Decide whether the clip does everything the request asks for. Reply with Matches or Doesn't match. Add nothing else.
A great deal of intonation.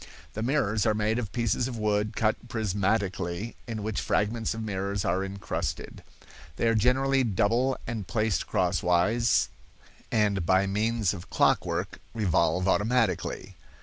Doesn't match